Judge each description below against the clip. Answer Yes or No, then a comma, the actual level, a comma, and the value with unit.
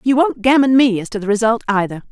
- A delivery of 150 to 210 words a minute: No, fast, 255 wpm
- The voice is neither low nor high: No, high, 230 Hz